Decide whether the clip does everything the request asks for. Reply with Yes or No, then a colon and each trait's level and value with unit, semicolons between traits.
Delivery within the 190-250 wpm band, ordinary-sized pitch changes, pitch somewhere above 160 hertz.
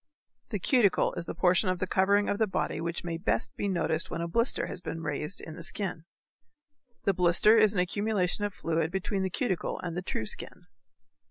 Yes: fast, 205 wpm; average, 3.2 semitones; medium, 185 Hz